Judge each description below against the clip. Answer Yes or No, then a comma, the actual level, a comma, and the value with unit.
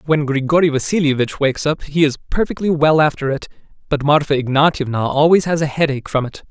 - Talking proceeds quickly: No, average, 195 wpm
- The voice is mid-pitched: Yes, medium, 145 Hz